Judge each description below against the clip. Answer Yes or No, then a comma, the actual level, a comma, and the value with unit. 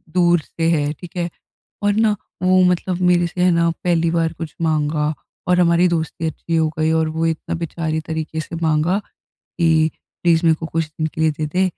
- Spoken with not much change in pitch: Yes, narrow, 1.6 semitones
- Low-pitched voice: No, medium, 165 Hz